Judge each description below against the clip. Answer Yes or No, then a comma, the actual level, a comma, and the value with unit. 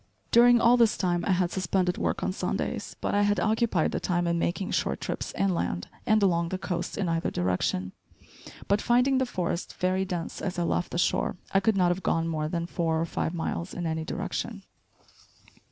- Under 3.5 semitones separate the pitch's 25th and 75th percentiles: Yes, average, 3.0 semitones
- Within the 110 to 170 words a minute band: No, average, 200 wpm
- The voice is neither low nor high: Yes, medium, 180 Hz